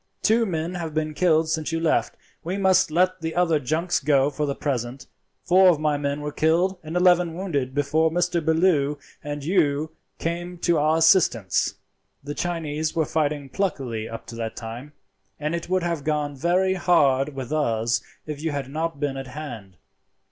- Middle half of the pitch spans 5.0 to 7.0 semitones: No, average, 3.4 semitones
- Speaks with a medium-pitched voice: Yes, medium, 155 Hz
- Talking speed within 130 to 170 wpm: No, average, 180 wpm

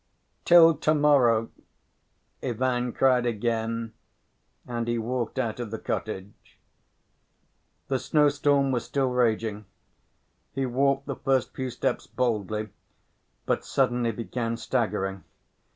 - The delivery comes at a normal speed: No, slow, 105 wpm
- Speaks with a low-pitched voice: Yes, low, 120 Hz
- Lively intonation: No, average, 2.8 semitones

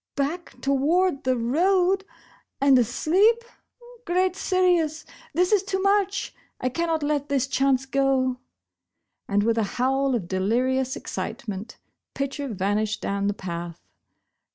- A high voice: Yes, very high, 275 Hz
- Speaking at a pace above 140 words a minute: No, slow, 135 wpm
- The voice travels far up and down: Yes, wide, 6.9 semitones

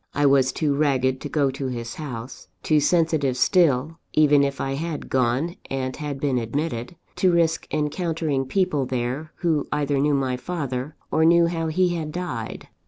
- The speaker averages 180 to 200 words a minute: No, average, 170 wpm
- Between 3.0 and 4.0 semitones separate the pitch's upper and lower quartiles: Yes, average, 3.7 semitones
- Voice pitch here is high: No, medium, 145 Hz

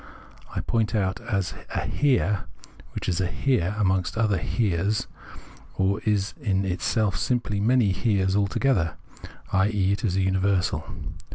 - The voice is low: Yes, low, 100 Hz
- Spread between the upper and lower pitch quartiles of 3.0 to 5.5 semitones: No, narrow, 2.6 semitones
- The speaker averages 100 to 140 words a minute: Yes, slow, 135 wpm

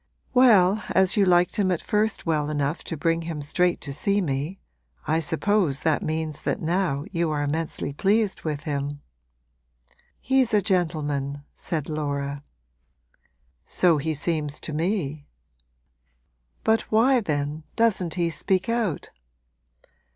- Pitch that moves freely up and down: No, average, 4.6 semitones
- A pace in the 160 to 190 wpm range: No, slow, 135 wpm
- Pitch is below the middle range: No, medium, 165 Hz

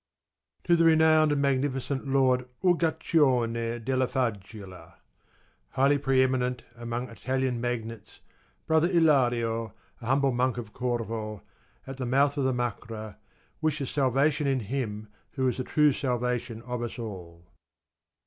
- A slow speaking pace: Yes, slow, 130 wpm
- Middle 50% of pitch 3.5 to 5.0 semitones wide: No, average, 3.1 semitones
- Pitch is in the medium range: No, low, 125 Hz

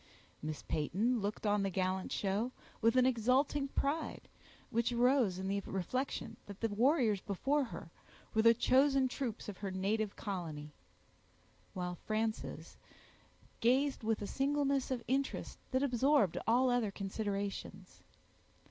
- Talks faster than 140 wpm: No, slow, 135 wpm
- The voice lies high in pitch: Yes, high, 225 Hz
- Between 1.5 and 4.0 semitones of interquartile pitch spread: No, average, 4.8 semitones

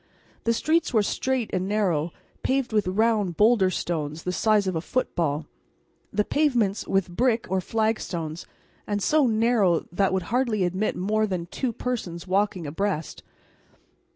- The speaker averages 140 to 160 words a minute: Yes, average, 155 wpm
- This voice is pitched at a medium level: No, high, 200 Hz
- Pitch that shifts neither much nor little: Yes, average, 4.3 semitones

